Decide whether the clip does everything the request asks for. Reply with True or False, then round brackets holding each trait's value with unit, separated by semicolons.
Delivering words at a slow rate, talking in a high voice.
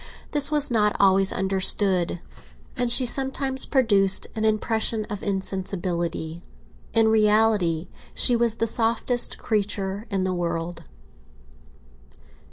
True (110 wpm; 210 Hz)